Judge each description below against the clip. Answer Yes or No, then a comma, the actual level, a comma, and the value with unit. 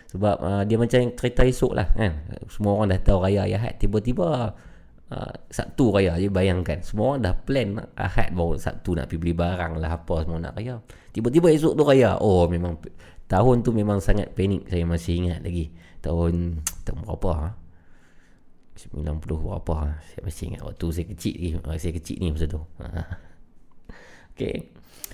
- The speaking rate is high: Yes, fast, 165 wpm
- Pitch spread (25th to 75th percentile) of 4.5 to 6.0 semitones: No, average, 4.0 semitones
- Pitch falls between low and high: No, very low, 90 Hz